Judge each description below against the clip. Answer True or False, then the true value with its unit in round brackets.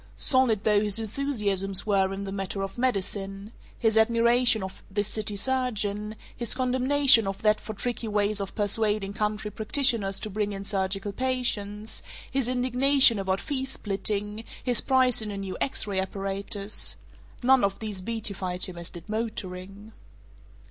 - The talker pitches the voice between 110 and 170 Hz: False (210 Hz)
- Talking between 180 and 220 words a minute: False (155 wpm)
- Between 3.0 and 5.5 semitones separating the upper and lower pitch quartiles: True (3.4 semitones)